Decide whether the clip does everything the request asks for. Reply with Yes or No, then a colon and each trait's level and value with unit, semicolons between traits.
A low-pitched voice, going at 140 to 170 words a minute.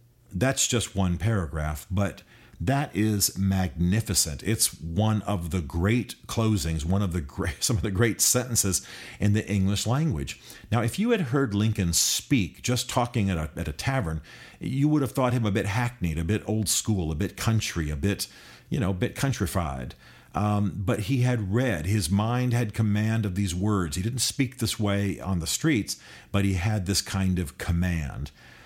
No: low, 105 Hz; average, 190 wpm